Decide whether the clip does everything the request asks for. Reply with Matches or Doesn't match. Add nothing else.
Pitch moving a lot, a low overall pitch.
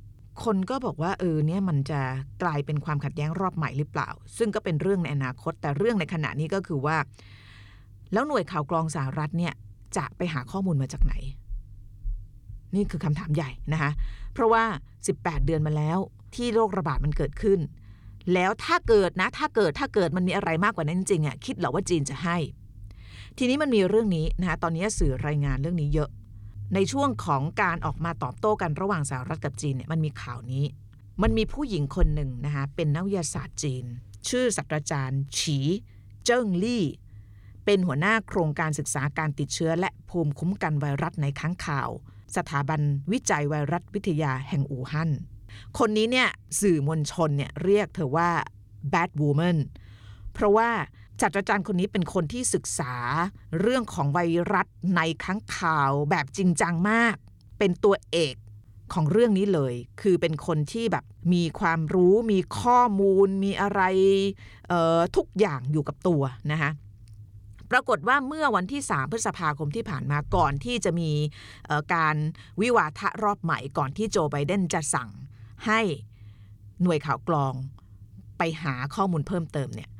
Doesn't match